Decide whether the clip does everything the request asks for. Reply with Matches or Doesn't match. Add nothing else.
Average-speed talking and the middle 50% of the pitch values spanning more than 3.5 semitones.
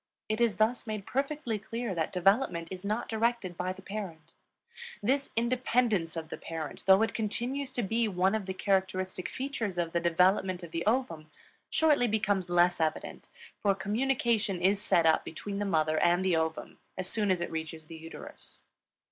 Matches